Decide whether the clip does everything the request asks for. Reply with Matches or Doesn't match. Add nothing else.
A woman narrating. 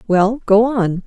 Matches